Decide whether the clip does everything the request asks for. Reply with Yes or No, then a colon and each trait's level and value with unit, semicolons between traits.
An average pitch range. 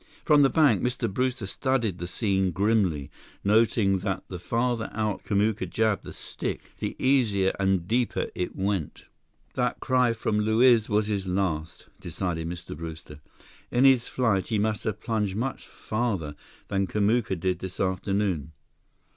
Yes: average, 3.7 semitones